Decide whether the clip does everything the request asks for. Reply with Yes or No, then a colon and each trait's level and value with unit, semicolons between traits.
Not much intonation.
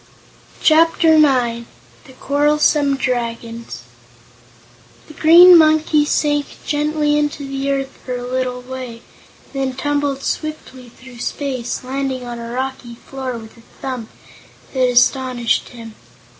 No: average, 3.1 semitones